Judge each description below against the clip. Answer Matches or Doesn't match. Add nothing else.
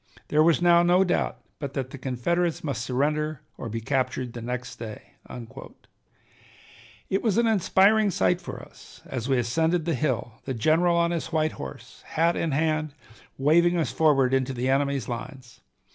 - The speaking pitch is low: Doesn't match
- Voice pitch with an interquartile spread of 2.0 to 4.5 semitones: Doesn't match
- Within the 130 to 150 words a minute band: Doesn't match